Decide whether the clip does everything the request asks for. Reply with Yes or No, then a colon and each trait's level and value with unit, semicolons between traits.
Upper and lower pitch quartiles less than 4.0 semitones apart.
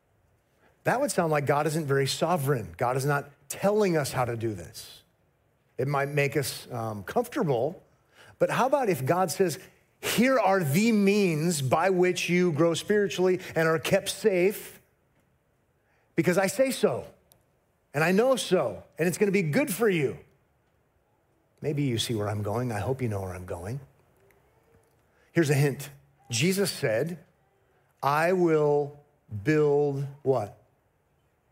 No: wide, 5.5 semitones